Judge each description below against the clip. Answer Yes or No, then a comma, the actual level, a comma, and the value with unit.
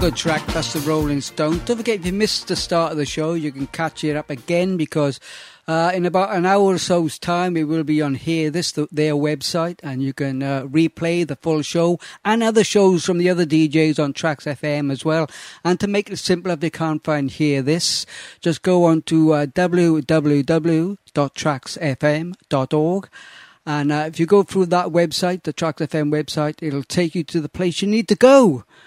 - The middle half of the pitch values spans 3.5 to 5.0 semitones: No, average, 2.9 semitones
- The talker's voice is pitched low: No, medium, 160 Hz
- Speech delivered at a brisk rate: Yes, fast, 215 wpm